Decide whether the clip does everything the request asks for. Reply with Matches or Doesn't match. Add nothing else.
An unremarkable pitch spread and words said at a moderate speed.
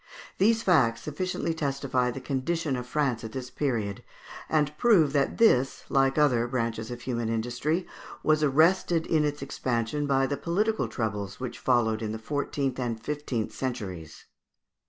Matches